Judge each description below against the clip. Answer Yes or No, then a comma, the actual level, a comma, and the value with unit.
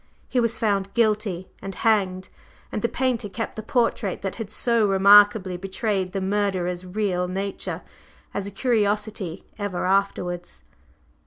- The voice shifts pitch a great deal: No, narrow, 2.5 semitones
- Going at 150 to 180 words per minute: No, average, 140 wpm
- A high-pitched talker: Yes, high, 200 Hz